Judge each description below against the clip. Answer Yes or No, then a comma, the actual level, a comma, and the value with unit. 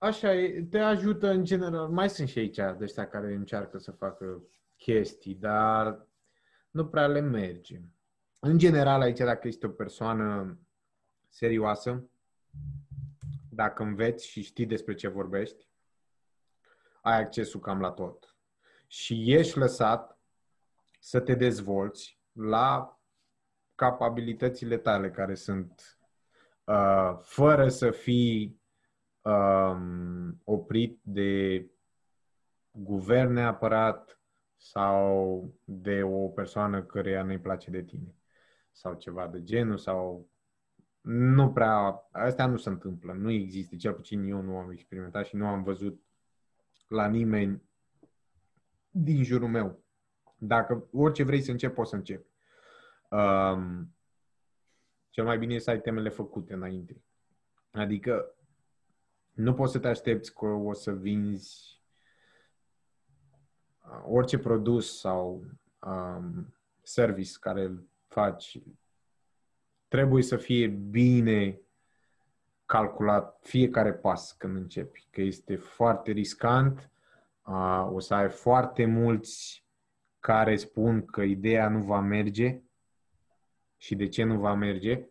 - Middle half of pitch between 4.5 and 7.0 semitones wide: No, average, 3.9 semitones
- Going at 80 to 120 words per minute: Yes, slow, 115 wpm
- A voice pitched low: Yes, low, 110 Hz